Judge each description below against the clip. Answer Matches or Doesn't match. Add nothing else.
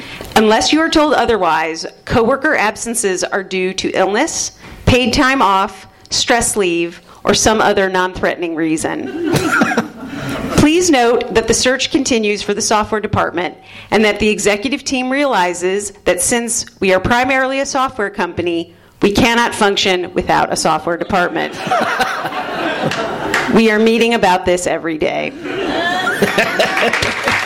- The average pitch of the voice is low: Doesn't match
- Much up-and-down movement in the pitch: Matches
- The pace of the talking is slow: Matches